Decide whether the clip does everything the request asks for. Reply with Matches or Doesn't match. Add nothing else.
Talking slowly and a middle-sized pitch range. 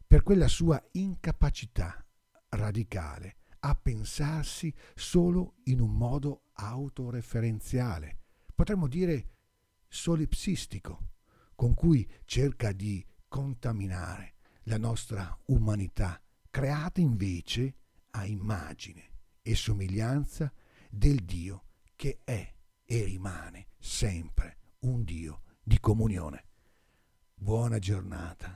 Doesn't match